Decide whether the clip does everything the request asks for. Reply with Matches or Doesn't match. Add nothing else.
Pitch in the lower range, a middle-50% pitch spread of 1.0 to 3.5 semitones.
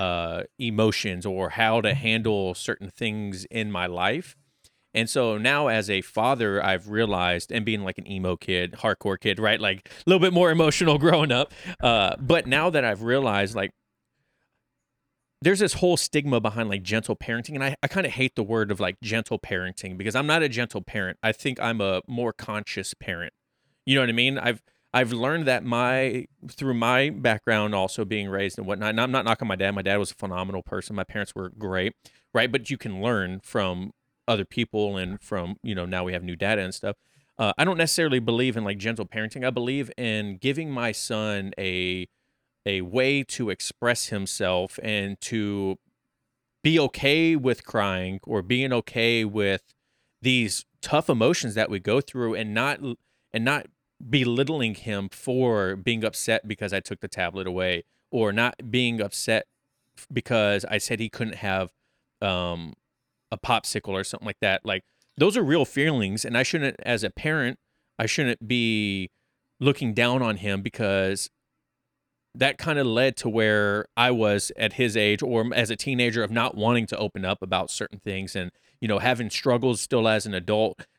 Doesn't match